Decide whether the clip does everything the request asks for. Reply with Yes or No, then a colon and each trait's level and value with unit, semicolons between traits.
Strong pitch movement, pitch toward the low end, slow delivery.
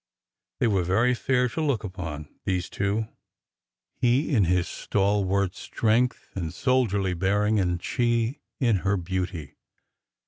No: average, 4.5 semitones; low, 100 Hz; slow, 130 wpm